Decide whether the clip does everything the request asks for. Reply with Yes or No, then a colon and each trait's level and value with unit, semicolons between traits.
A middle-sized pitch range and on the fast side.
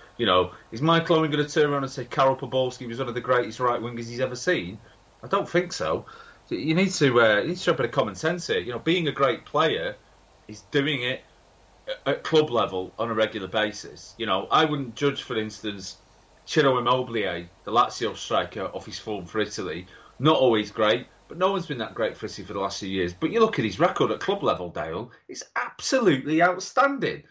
No: wide, 6.4 semitones; fast, 220 wpm